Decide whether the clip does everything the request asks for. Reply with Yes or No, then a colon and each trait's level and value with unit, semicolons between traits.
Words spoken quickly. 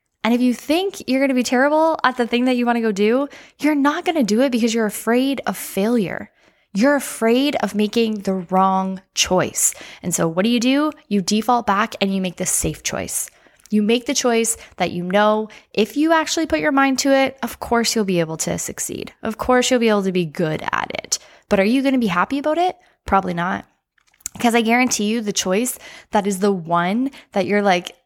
Yes: fast, 220 wpm